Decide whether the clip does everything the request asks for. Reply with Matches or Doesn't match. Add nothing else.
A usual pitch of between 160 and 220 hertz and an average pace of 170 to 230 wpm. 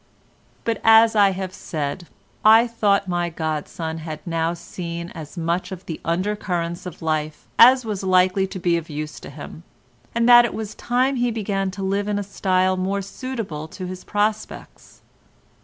Matches